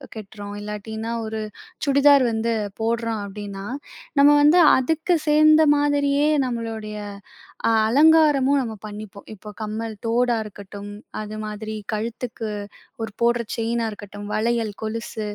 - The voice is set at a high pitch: Yes, high, 225 Hz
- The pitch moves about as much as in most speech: Yes, average, 4.4 semitones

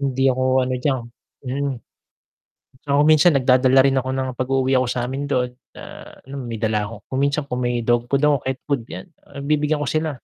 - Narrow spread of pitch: Yes, narrow, 2.1 semitones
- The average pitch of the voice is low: Yes, low, 130 Hz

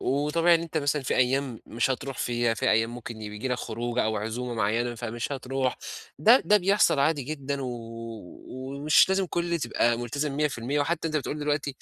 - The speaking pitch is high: No, low, 135 Hz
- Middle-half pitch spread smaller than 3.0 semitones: No, average, 4.0 semitones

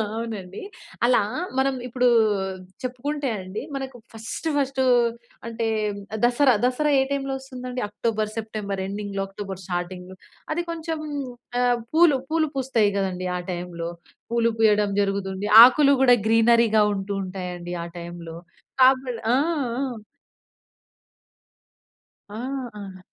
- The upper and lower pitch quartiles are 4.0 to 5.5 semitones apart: Yes, average, 5.0 semitones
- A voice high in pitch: Yes, high, 225 Hz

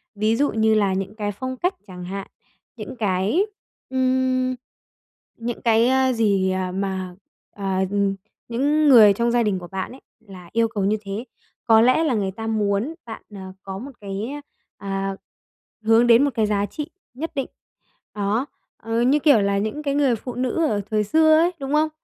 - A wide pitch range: No, average, 4.6 semitones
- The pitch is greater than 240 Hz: No, high, 225 Hz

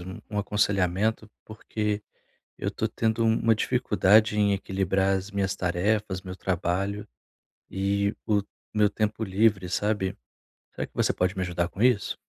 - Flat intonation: Yes, narrow, 2.2 semitones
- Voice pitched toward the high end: No, low, 100 Hz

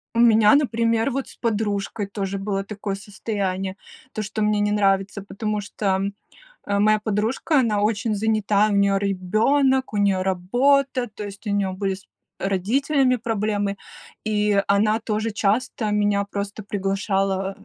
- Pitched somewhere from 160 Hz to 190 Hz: No, high, 210 Hz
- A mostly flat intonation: Yes, narrow, 2.0 semitones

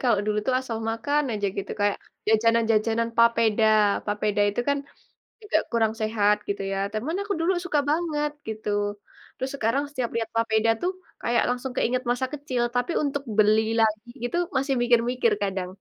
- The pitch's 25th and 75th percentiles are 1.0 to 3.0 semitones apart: No, average, 3.5 semitones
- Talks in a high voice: Yes, high, 230 Hz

